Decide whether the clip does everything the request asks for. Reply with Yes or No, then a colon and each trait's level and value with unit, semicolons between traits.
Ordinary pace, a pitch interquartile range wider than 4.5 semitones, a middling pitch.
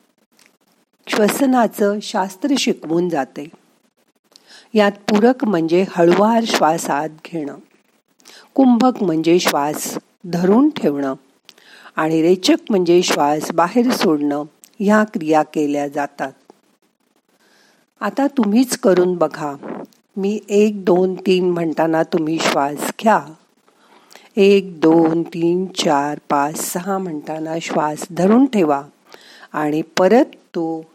Yes: average, 95 wpm; average, 5.1 semitones; medium, 180 Hz